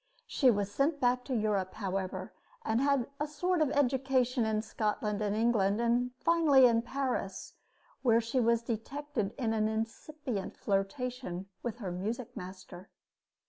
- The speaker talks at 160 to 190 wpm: No, average, 145 wpm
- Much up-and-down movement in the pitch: No, average, 4.1 semitones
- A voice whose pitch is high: Yes, high, 235 Hz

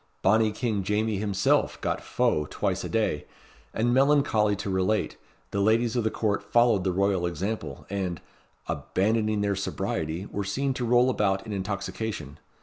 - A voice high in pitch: No, low, 105 Hz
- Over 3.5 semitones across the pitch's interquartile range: No, narrow, 2.6 semitones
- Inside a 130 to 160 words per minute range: Yes, average, 155 wpm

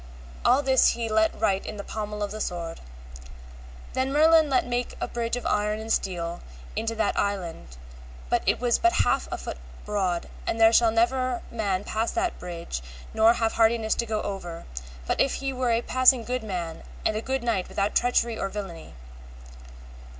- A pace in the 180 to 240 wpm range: Yes, average, 185 wpm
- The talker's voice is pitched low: No, high, 220 Hz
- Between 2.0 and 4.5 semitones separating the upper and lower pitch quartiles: Yes, average, 3.8 semitones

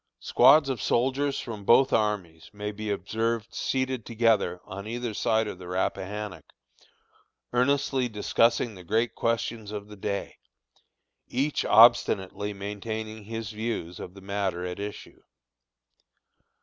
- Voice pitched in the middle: No, low, 110 Hz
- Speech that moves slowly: Yes, slow, 125 wpm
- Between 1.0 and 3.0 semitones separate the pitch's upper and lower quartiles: Yes, average, 2.7 semitones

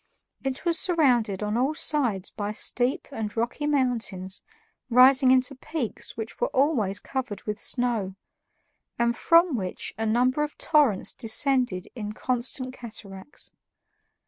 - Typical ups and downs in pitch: Yes, average, 4.3 semitones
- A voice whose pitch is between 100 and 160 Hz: No, high, 245 Hz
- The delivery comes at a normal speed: No, slow, 130 wpm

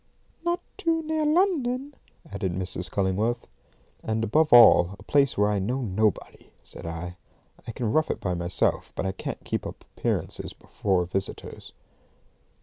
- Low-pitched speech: Yes, low, 110 Hz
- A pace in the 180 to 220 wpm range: No, average, 150 wpm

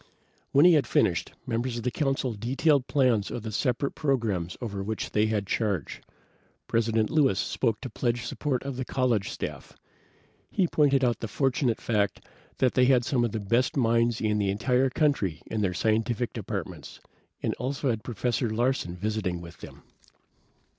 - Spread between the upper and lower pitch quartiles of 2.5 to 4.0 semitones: Yes, average, 3.5 semitones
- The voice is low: Yes, low, 120 Hz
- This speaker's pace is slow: No, average, 170 wpm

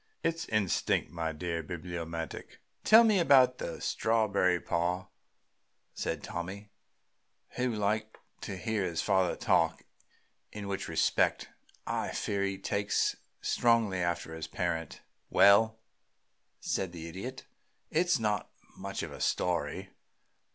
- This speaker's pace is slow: Yes, slow, 115 wpm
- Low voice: Yes, low, 100 Hz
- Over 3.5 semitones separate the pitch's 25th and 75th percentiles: Yes, average, 4.2 semitones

